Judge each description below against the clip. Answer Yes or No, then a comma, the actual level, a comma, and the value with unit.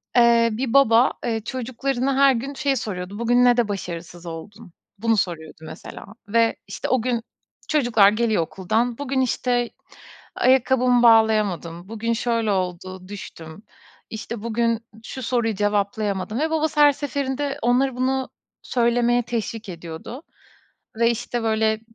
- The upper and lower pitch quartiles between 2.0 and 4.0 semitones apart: Yes, average, 3.4 semitones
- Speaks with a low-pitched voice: No, high, 230 Hz